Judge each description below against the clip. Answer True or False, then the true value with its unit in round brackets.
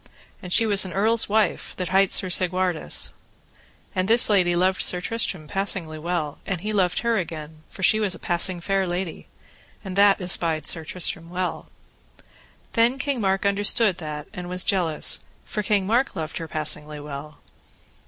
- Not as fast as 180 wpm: True (170 wpm)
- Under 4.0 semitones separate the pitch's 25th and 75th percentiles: True (3.2 semitones)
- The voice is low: False (185 Hz)